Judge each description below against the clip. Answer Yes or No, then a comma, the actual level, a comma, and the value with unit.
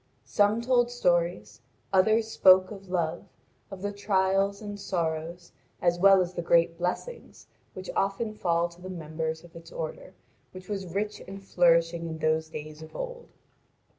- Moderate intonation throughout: Yes, average, 3.1 semitones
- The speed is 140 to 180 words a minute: Yes, average, 165 wpm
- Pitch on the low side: No, medium, 185 Hz